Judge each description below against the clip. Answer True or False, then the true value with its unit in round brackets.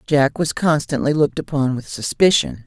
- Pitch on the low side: False (145 Hz)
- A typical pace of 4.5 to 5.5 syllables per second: True (5.1 syllables/s)